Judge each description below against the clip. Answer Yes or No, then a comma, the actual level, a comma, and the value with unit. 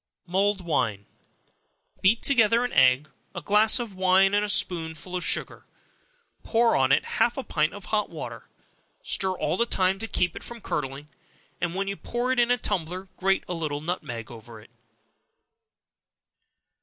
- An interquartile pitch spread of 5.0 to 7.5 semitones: Yes, wide, 5.4 semitones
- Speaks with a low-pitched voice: No, high, 190 Hz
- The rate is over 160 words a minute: Yes, average, 170 wpm